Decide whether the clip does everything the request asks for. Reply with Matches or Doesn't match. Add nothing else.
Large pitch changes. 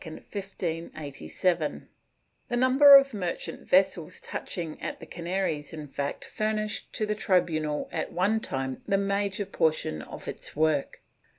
Doesn't match